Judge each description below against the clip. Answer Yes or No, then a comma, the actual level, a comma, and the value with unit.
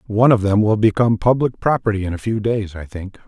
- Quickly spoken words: Yes, fast, 240 wpm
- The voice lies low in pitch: Yes, low, 105 Hz